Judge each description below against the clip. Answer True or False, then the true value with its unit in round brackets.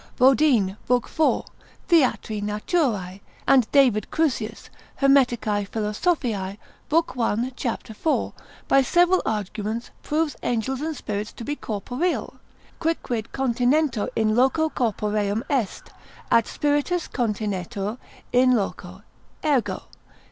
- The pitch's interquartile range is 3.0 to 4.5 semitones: False (5.1 semitones)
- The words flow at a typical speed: False (105 wpm)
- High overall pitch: True (240 Hz)